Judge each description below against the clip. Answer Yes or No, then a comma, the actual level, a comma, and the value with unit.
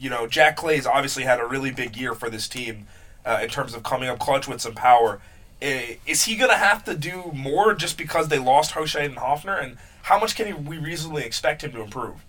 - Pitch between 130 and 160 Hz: Yes, medium, 140 Hz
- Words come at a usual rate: No, fast, 235 wpm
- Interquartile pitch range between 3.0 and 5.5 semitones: Yes, average, 4.9 semitones